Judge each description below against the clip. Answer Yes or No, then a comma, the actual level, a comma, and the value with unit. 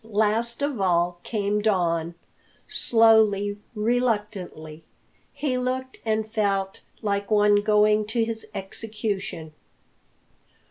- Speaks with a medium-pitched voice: No, high, 210 Hz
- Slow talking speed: Yes, slow, 95 wpm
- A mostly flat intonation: Yes, narrow, 2.3 semitones